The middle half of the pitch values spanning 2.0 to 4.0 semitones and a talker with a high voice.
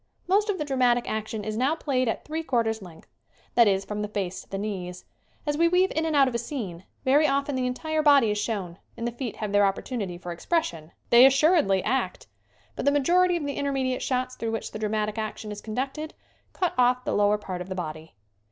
No: wide, 5.6 semitones; high, 240 Hz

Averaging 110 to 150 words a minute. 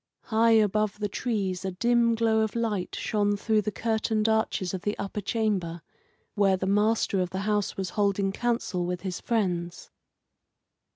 No: average, 165 wpm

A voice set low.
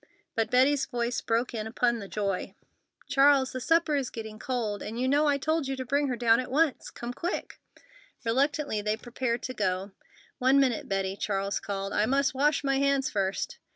No: very high, 250 Hz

